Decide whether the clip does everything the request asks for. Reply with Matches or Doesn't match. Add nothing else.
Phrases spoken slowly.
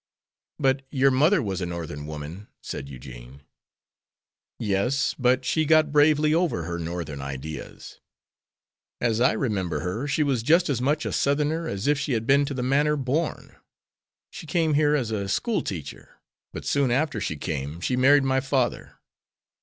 Doesn't match